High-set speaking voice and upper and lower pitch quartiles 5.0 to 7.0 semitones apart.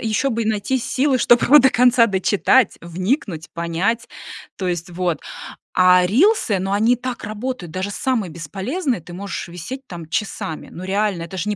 Yes: high, 205 Hz; wide, 5.6 semitones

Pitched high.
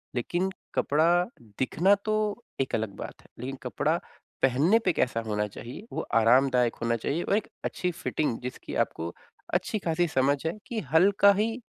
No: medium, 155 Hz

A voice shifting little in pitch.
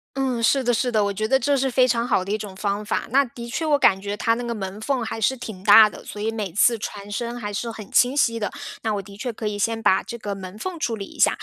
No: average, 3.1 semitones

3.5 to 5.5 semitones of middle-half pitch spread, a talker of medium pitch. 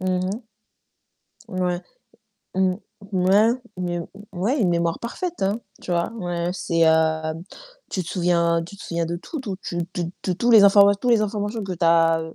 No: average, 3.0 semitones; medium, 180 Hz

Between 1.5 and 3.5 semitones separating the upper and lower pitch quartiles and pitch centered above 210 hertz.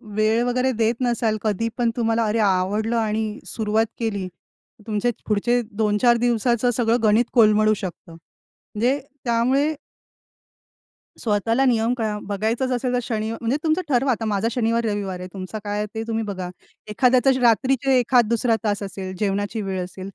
Yes: narrow, 2.6 semitones; high, 225 Hz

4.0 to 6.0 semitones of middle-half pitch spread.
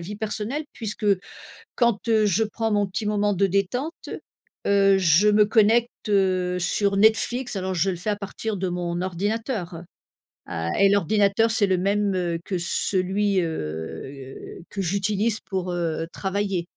No: average, 2.7 semitones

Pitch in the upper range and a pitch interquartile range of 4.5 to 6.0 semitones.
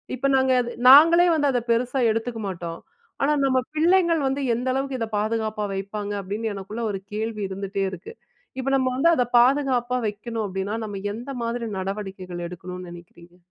Yes: high, 225 Hz; average, 5.0 semitones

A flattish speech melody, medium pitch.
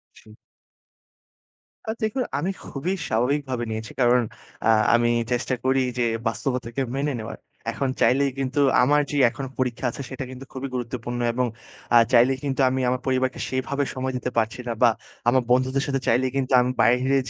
No: narrow, 1.9 semitones; low, 130 Hz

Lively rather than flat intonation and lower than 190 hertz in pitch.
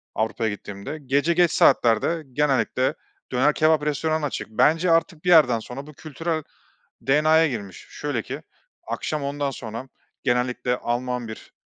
No: average, 4.2 semitones; medium, 140 Hz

